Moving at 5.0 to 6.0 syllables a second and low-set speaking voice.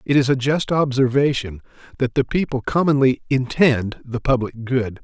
No: 4.8 syllables/s; low, 130 Hz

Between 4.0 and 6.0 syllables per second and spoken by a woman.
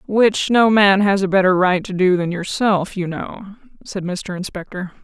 Yes: 4.5 syllables/s; female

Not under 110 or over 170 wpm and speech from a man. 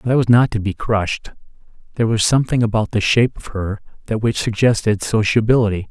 No: average, 195 wpm; male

